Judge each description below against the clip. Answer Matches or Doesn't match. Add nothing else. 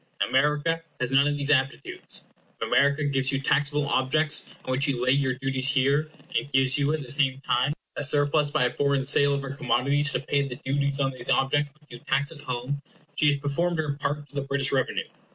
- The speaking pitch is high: Doesn't match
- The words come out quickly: Matches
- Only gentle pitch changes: Matches